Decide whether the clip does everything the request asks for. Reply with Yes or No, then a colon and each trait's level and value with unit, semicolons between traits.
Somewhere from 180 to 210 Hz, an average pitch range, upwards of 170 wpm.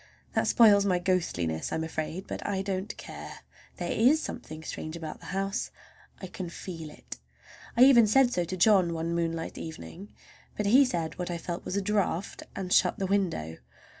Yes: medium, 185 Hz; average, 3.5 semitones; average, 180 wpm